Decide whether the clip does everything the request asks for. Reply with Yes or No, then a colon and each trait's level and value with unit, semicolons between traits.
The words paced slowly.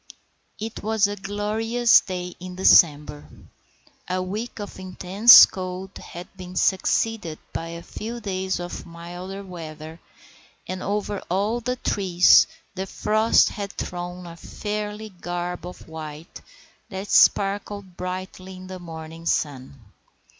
Yes: slow, 125 wpm